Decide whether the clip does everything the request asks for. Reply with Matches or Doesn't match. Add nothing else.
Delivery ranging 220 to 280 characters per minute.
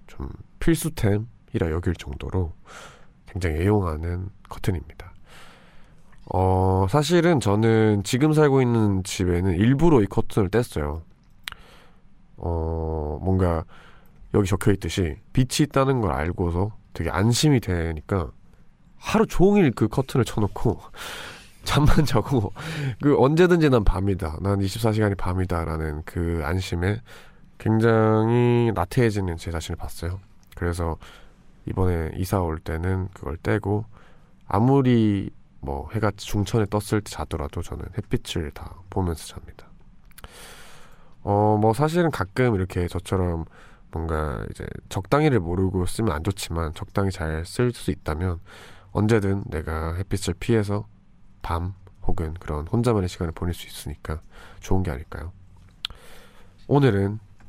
Matches